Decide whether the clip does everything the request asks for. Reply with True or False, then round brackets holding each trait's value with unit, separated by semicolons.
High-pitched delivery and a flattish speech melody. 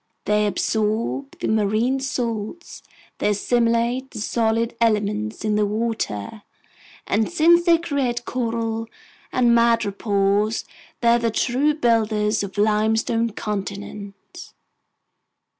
True (225 Hz; 2.2 semitones)